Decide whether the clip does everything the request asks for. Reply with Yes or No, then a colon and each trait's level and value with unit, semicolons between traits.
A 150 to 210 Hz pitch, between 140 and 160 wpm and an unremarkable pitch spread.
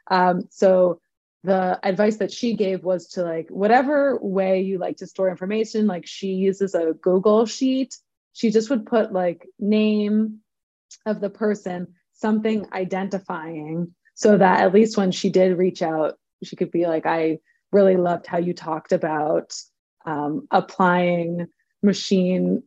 Yes: high, 190 Hz; average, 150 wpm; average, 3.0 semitones